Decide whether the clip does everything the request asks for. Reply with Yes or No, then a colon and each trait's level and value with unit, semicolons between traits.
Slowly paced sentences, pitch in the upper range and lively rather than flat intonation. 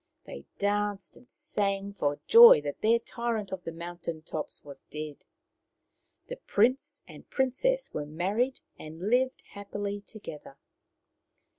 Yes: slow, 130 wpm; high, 200 Hz; wide, 6.5 semitones